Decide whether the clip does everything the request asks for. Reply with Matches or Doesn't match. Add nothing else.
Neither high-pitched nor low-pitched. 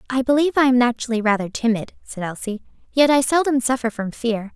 Doesn't match